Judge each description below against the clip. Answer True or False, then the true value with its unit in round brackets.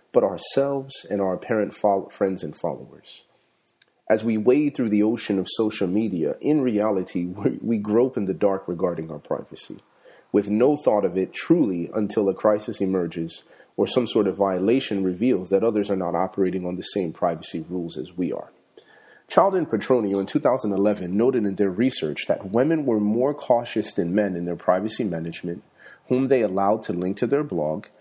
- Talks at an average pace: True (180 wpm)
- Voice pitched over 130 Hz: False (100 Hz)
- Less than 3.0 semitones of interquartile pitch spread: False (3.4 semitones)